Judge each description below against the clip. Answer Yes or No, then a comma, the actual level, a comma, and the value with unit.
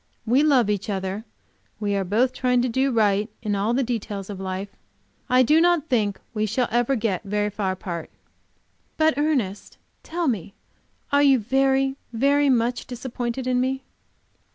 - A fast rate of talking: No, average, 165 wpm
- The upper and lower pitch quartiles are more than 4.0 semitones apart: Yes, average, 4.6 semitones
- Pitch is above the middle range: Yes, high, 240 Hz